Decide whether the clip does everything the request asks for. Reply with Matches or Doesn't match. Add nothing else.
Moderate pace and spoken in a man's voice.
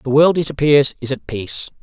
Doesn't match